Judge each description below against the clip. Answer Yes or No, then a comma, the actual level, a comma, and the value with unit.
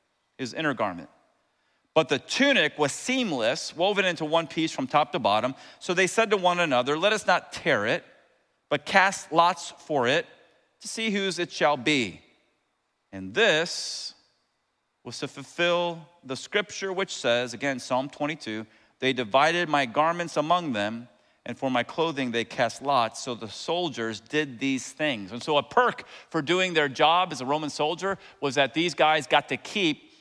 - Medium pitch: Yes, medium, 155 Hz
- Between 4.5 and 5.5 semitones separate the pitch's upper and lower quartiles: Yes, average, 5.2 semitones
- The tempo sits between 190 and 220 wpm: No, average, 175 wpm